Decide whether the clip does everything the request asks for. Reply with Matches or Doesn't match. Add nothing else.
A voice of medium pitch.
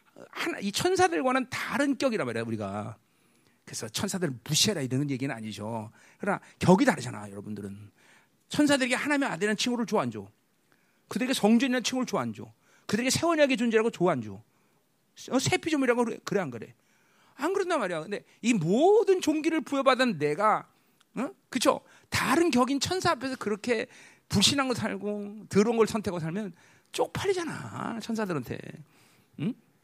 Doesn't match